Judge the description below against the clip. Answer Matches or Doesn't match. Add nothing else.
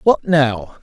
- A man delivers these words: Matches